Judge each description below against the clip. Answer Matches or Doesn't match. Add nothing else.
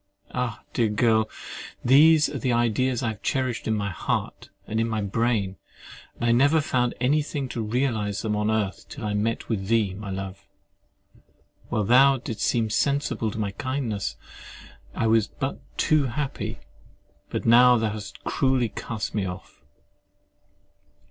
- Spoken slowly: Doesn't match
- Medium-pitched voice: Doesn't match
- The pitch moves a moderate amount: Matches